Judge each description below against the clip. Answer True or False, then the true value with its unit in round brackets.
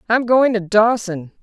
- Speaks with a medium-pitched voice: False (215 Hz)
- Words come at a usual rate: True (170 wpm)